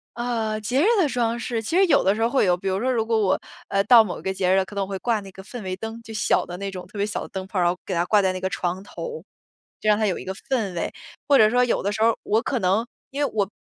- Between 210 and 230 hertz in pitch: Yes, high, 215 Hz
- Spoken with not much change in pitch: No, average, 3.5 semitones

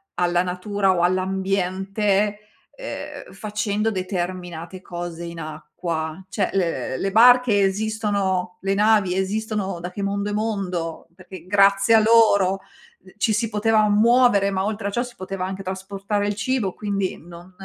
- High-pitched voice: Yes, high, 195 Hz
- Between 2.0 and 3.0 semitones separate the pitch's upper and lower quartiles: Yes, narrow, 2.4 semitones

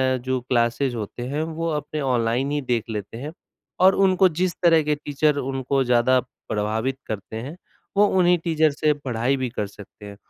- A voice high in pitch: No, low, 135 Hz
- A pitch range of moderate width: Yes, average, 4.5 semitones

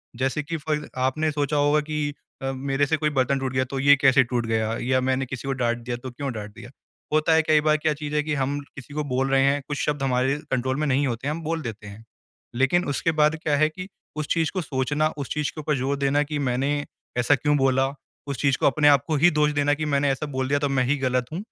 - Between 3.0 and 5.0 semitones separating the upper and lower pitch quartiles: No, narrow, 2.4 semitones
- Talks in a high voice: No, medium, 140 Hz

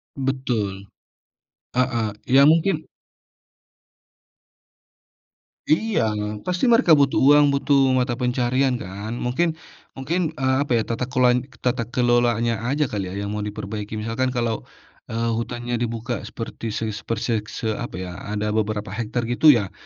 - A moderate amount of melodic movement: Yes, average, 3.4 semitones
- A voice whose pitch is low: Yes, low, 120 Hz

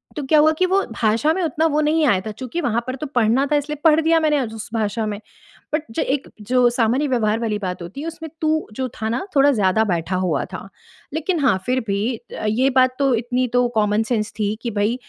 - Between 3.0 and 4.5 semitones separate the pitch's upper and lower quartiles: No, wide, 5.6 semitones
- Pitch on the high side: Yes, high, 245 Hz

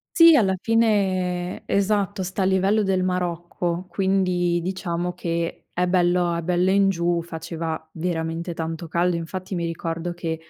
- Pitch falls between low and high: Yes, medium, 180 Hz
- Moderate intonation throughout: No, narrow, 2.0 semitones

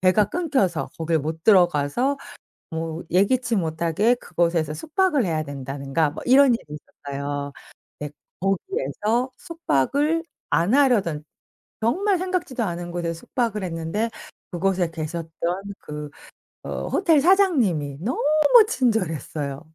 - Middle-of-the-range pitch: Yes, medium, 180 Hz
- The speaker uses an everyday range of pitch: No, wide, 8.1 semitones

